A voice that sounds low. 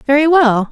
No: very high, 275 Hz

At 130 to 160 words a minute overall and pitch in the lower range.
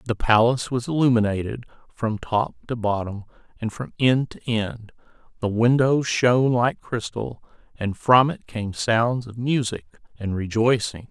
Yes: average, 145 wpm; low, 115 Hz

